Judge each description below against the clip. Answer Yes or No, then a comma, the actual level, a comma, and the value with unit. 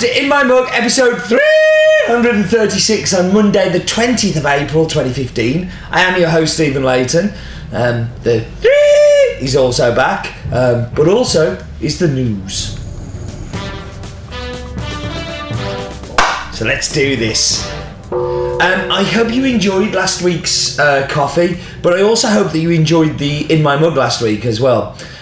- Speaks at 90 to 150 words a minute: Yes, average, 140 wpm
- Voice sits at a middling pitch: Yes, medium, 160 Hz